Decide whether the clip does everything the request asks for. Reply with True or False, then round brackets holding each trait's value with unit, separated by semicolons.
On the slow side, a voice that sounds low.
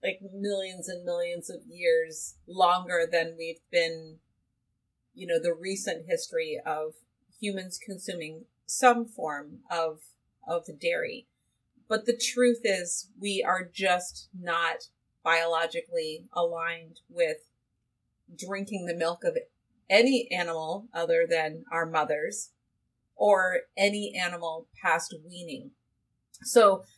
False (110 wpm; 180 Hz)